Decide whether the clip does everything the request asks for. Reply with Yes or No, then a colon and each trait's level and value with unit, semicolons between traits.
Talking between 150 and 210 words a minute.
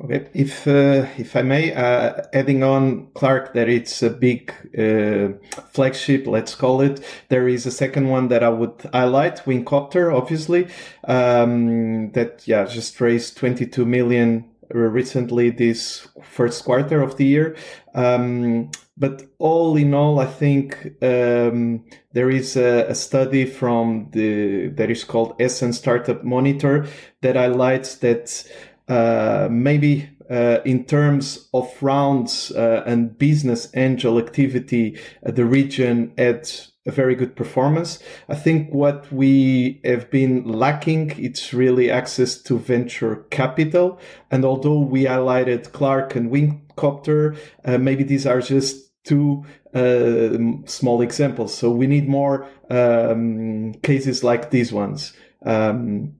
No: slow, 135 wpm